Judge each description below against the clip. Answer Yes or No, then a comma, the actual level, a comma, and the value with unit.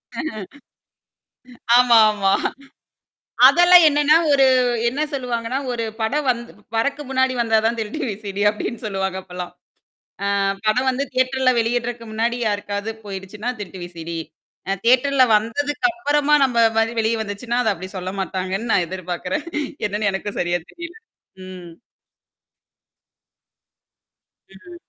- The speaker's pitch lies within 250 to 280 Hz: No, high, 230 Hz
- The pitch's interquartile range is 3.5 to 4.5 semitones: No, average, 5.0 semitones